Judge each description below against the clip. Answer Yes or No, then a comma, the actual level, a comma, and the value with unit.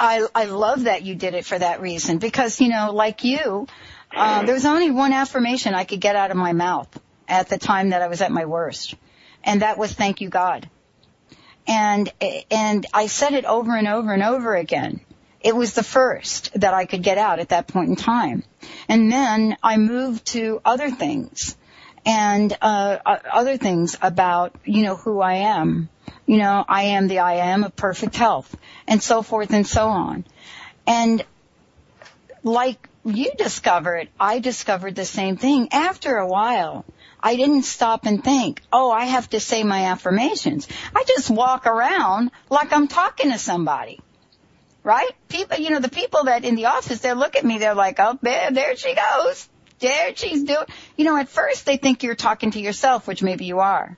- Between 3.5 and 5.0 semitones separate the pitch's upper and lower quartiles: Yes, average, 4.6 semitones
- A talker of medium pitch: No, high, 220 Hz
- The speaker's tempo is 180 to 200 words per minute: Yes, average, 190 wpm